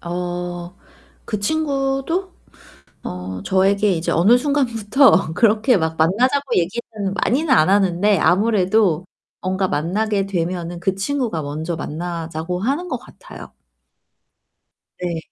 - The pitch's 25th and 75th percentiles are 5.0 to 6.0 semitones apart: Yes, wide, 5.5 semitones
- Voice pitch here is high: Yes, high, 195 Hz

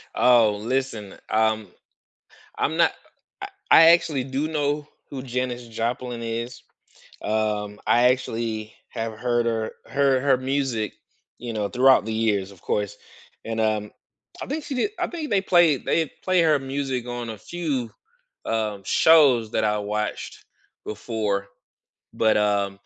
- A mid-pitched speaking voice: No, low, 120 Hz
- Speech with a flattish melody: No, average, 3.8 semitones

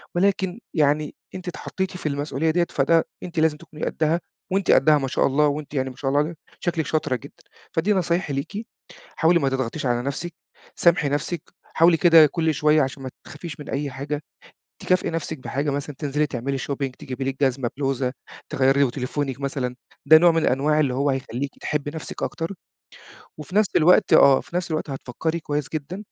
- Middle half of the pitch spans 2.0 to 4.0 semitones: Yes, average, 3.3 semitones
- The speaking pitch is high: No, medium, 150 Hz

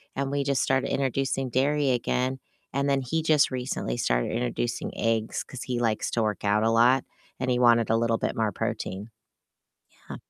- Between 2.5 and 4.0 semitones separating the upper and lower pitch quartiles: Yes, average, 2.9 semitones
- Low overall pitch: Yes, low, 125 Hz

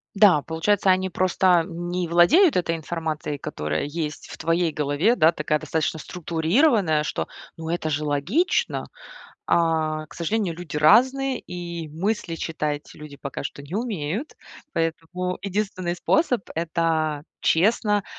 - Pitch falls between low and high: Yes, medium, 170 Hz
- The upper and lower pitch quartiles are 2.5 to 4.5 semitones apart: Yes, average, 3.4 semitones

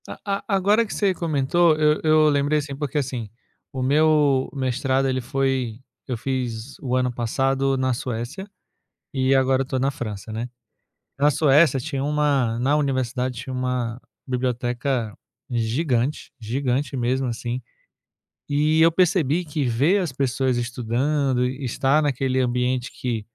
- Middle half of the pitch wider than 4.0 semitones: No, average, 2.9 semitones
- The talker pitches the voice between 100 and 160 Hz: Yes, low, 135 Hz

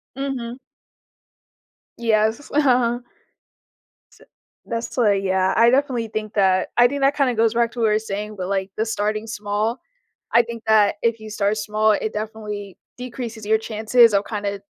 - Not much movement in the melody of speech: Yes, narrow, 2.1 semitones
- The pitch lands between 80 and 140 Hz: No, high, 220 Hz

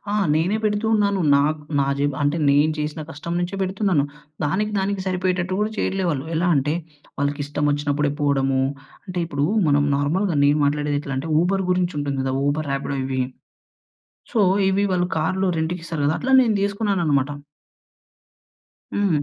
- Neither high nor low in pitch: Yes, medium, 155 Hz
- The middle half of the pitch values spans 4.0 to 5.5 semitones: Yes, average, 4.8 semitones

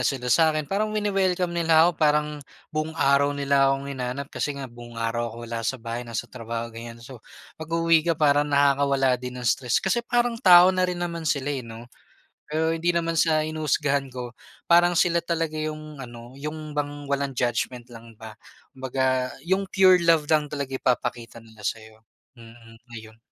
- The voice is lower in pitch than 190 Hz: Yes, medium, 140 Hz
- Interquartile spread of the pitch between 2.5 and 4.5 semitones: No, average, 5.1 semitones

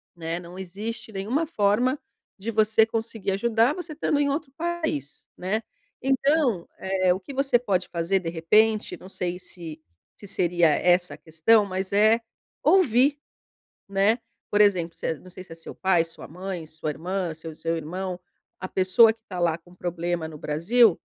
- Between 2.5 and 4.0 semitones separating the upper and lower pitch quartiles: No, average, 4.7 semitones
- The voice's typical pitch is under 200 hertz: Yes, high, 190 Hz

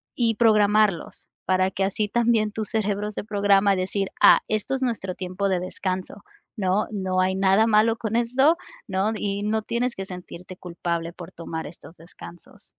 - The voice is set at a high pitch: Yes, high, 200 Hz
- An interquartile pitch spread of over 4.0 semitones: No, average, 2.8 semitones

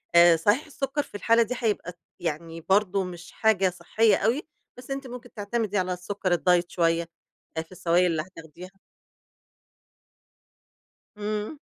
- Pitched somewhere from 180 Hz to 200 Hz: Yes, high, 190 Hz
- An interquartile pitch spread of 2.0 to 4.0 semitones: No, average, 4.5 semitones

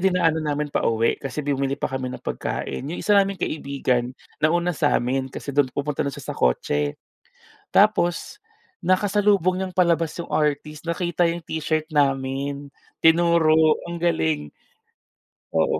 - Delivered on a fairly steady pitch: No, average, 4.2 semitones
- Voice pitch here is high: No, medium, 155 Hz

